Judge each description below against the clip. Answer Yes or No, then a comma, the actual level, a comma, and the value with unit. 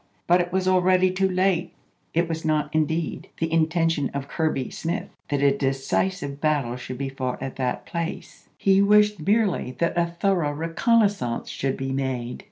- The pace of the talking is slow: No, average, 190 wpm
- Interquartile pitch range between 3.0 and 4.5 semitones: No, average, 5.1 semitones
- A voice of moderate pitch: Yes, medium, 160 Hz